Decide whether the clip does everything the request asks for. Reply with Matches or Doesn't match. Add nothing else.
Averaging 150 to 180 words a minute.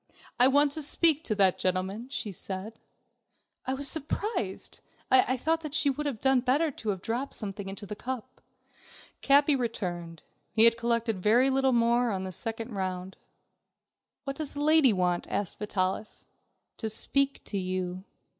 Matches